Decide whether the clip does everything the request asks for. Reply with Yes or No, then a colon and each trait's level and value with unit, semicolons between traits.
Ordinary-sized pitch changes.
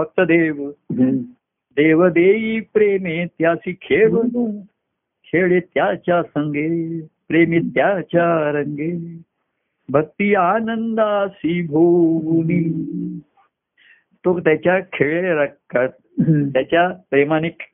Yes: average, 3.7 semitones